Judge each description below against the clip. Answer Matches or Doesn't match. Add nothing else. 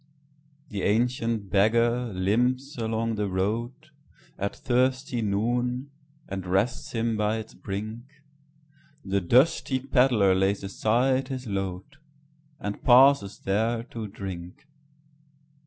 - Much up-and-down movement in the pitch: Doesn't match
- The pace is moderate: Doesn't match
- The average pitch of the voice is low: Matches